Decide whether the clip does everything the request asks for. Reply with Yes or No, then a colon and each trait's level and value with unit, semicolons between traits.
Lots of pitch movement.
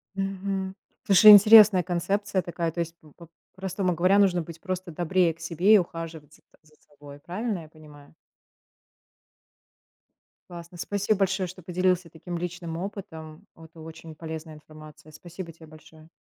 No: average, 2.9 semitones